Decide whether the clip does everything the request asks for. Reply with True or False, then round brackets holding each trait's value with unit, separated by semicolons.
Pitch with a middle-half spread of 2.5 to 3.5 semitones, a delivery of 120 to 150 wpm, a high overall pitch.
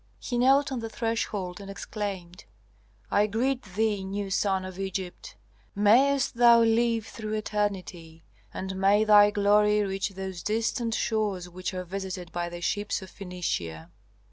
True (2.9 semitones; 145 wpm; 205 Hz)